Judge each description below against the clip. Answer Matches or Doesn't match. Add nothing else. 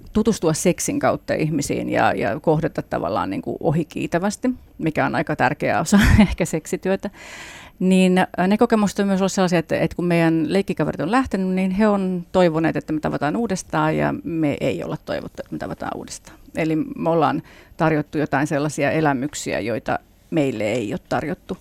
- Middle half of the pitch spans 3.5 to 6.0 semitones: Matches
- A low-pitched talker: Doesn't match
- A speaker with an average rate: Doesn't match